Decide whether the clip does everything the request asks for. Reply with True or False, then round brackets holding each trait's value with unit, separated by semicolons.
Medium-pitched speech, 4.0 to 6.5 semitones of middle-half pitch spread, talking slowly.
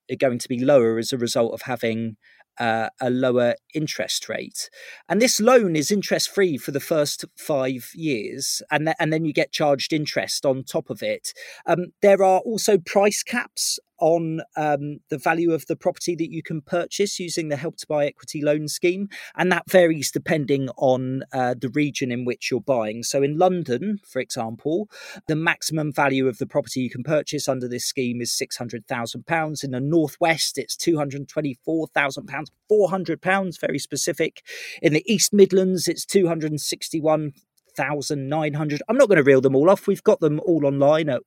False (155 Hz; 4.4 semitones; 175 wpm)